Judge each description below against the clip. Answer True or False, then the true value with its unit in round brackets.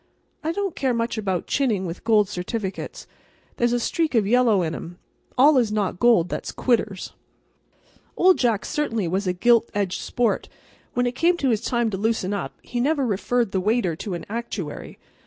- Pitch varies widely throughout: False (4.2 semitones)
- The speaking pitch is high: True (225 Hz)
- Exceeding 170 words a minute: True (180 wpm)